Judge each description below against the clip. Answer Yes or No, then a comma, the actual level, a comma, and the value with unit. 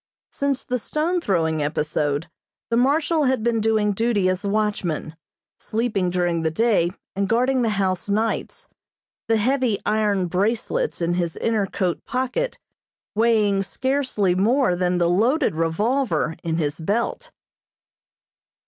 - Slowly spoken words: Yes, slow, 130 wpm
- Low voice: No, high, 210 Hz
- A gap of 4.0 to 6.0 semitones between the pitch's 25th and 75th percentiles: Yes, wide, 5.6 semitones